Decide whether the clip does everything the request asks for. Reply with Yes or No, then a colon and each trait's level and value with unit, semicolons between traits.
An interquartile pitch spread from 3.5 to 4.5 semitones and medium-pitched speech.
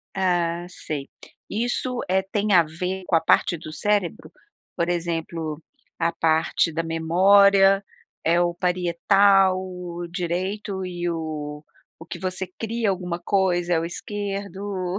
No: average, 2.7 semitones; medium, 180 Hz